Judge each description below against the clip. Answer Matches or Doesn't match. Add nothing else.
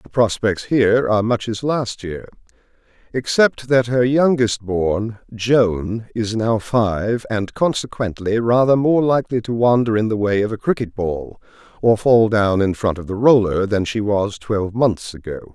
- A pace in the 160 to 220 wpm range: Matches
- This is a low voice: Matches